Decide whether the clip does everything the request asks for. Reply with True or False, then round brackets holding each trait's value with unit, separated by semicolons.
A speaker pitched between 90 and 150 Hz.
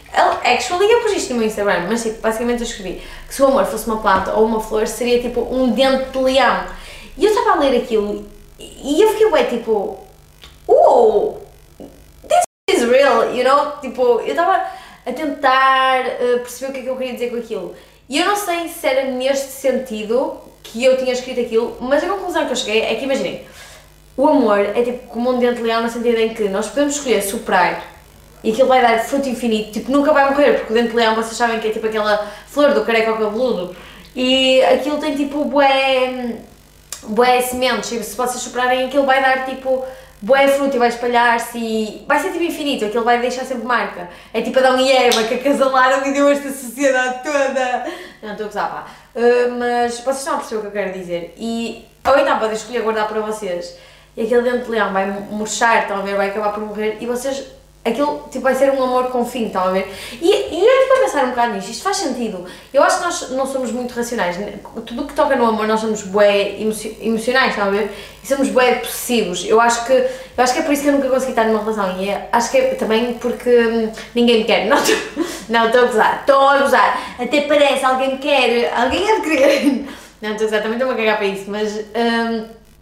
False (245 Hz)